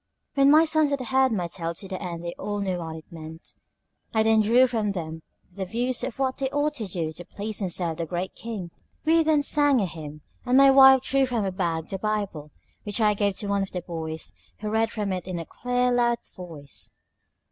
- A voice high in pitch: Yes, high, 205 Hz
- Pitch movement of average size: No, wide, 6.4 semitones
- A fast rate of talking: Yes, fast, 230 wpm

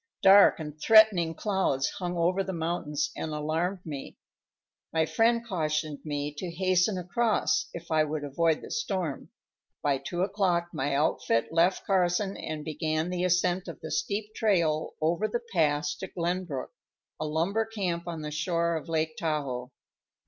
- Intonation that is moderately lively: Yes, average, 3.4 semitones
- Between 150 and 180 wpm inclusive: Yes, average, 160 wpm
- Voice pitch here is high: No, medium, 170 Hz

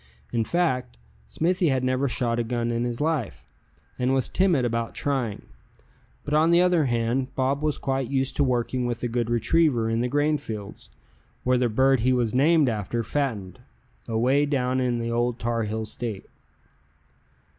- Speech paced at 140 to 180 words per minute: Yes, average, 170 wpm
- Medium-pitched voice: No, low, 125 Hz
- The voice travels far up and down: No, average, 3.1 semitones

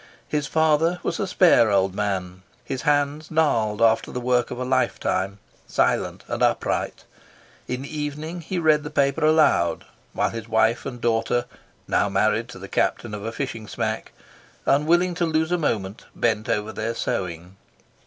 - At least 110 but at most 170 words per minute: Yes, average, 165 wpm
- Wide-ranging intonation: Yes, wide, 5.9 semitones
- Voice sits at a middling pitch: No, low, 125 Hz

